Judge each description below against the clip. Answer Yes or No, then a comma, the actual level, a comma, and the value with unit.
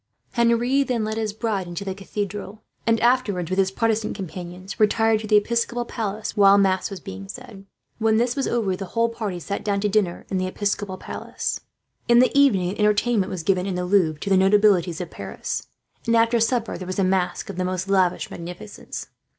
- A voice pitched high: Yes, high, 200 Hz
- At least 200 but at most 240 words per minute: Yes, fast, 205 wpm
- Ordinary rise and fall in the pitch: Yes, average, 3.2 semitones